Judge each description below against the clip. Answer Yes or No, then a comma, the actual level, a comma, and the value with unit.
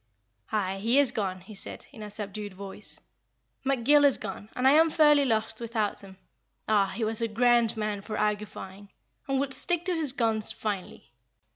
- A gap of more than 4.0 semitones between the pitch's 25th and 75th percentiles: Yes, average, 4.5 semitones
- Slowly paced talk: No, average, 180 wpm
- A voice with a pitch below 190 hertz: No, high, 220 Hz